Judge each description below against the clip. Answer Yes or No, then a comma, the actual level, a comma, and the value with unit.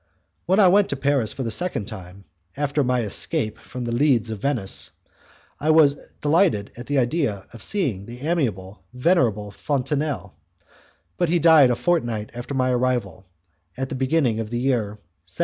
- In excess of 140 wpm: Yes, average, 175 wpm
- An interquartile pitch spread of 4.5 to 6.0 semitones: Yes, average, 5.2 semitones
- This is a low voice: Yes, low, 125 Hz